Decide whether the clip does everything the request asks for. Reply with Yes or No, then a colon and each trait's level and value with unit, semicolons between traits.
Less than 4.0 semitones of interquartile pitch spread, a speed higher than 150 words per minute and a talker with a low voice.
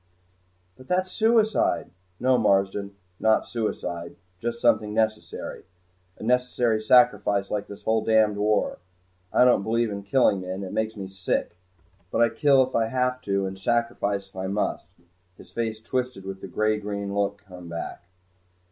Yes: average, 3.1 semitones; average, 160 wpm; low, 110 Hz